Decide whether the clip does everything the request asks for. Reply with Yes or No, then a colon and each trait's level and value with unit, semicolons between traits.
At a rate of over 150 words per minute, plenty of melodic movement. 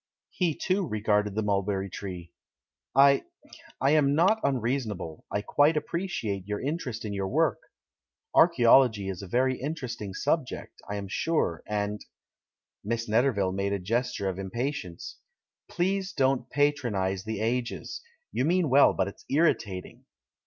No: average, 145 wpm; wide, 6.3 semitones